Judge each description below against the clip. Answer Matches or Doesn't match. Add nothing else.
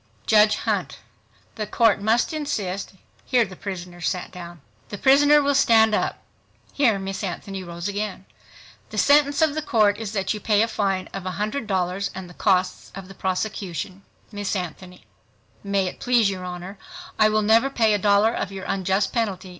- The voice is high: Matches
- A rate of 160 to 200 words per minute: Matches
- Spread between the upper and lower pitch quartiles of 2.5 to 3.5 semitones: Matches